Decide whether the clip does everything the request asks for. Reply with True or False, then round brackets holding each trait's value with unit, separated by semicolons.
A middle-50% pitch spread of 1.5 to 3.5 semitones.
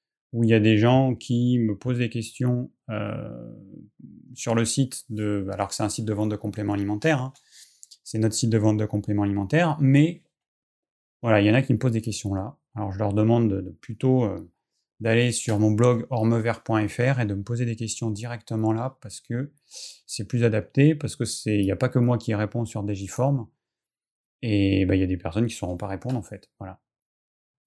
True (2.9 semitones)